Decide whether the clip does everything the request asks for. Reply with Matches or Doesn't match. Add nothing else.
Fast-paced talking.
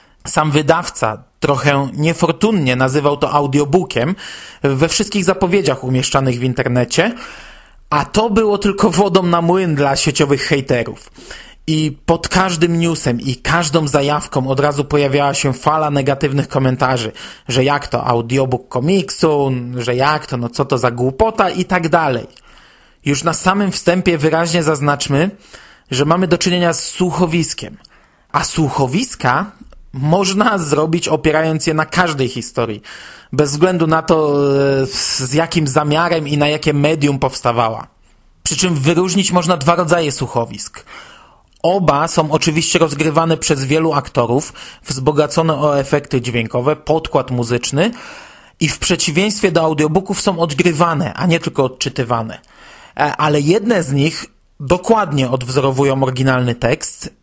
Doesn't match